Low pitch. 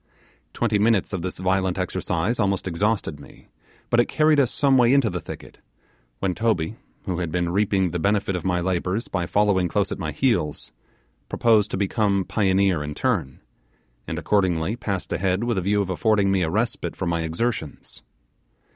Yes: very low, 95 Hz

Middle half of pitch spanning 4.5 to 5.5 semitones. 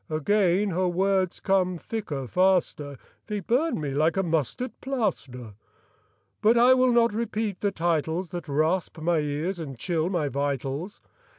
Yes: average, 5.1 semitones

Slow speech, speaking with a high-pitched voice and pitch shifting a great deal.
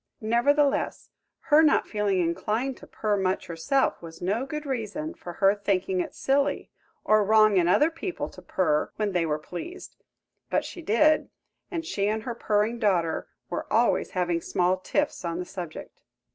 No: average, 170 wpm; high, 210 Hz; wide, 7.1 semitones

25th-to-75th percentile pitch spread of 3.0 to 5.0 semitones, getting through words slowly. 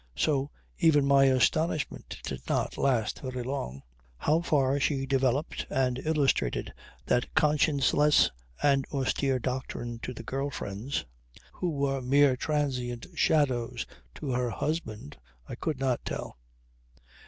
No: narrow, 2.6 semitones; slow, 125 wpm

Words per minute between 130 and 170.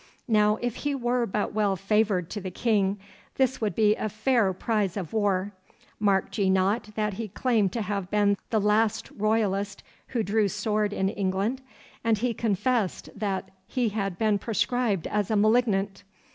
Yes: average, 165 wpm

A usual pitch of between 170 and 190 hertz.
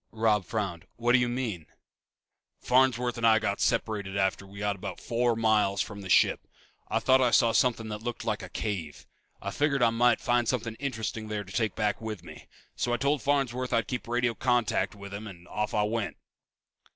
No: low, 110 Hz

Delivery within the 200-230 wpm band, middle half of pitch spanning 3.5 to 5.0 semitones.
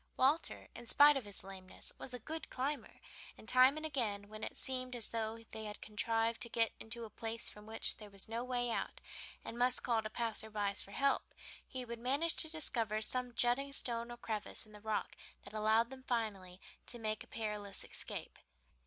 No: fast, 205 wpm; average, 2.8 semitones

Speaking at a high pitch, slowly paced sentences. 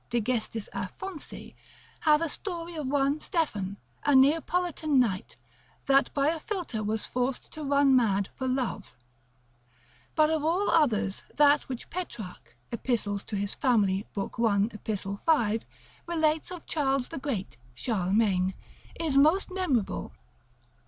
Yes: very high, 265 Hz; slow, 130 wpm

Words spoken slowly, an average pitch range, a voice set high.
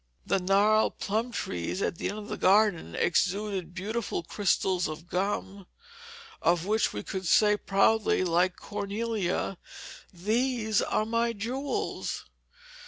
Yes: slow, 125 wpm; average, 3.1 semitones; high, 200 Hz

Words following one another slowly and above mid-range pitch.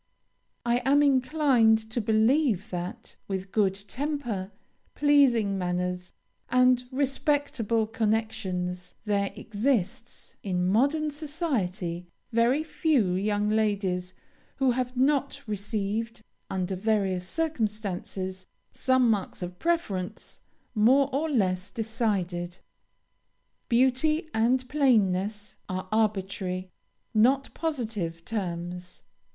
Yes: slow, 95 wpm; high, 220 Hz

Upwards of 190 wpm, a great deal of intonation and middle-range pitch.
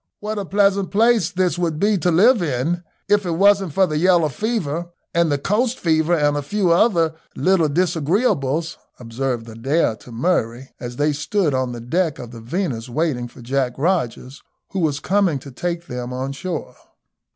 No: average, 180 wpm; wide, 5.9 semitones; medium, 165 Hz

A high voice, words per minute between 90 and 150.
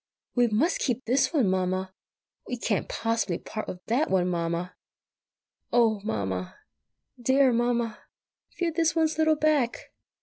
Yes: high, 230 Hz; slow, 135 wpm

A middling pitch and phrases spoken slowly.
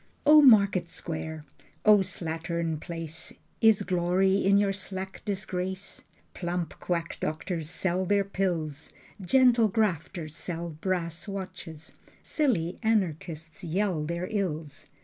Yes: medium, 180 Hz; slow, 110 wpm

